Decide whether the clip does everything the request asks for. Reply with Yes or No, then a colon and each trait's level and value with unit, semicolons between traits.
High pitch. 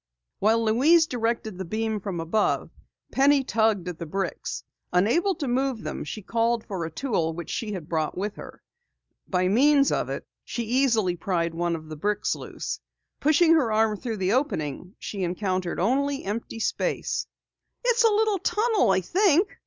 Yes: high, 220 Hz